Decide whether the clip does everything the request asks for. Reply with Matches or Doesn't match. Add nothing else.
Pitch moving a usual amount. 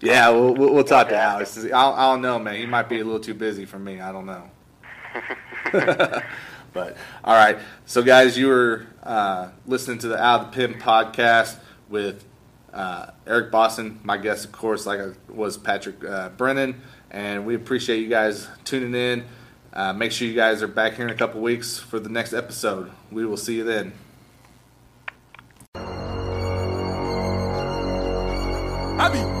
Matches